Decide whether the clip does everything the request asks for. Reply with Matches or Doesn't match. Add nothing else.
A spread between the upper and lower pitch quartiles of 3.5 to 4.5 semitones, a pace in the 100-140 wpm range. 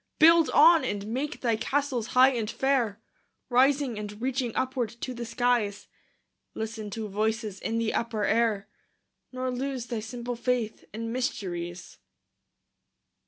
Doesn't match